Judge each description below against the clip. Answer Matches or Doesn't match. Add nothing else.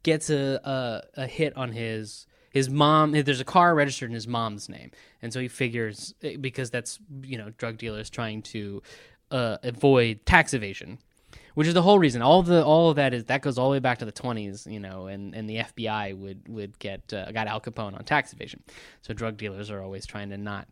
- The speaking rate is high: Matches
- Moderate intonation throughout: Matches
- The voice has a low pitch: Matches